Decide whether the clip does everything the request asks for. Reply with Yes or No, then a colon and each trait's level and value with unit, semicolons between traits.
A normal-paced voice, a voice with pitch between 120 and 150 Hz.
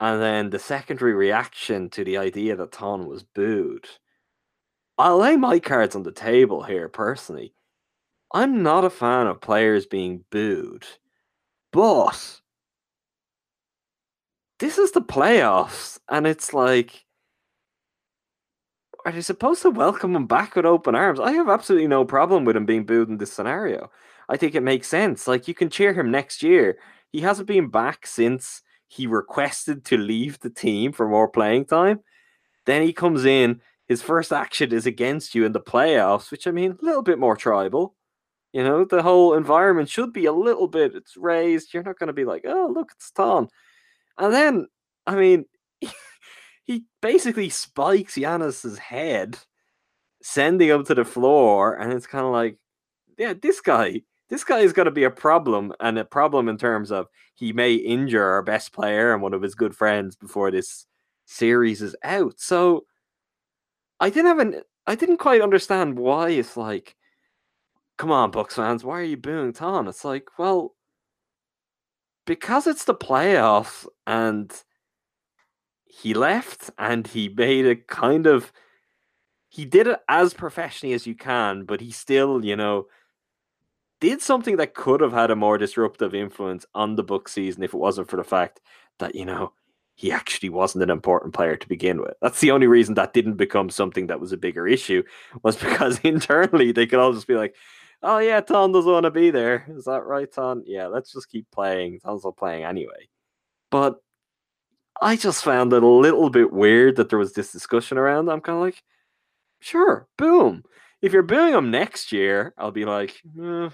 Yes: average, 180 wpm; medium, 140 Hz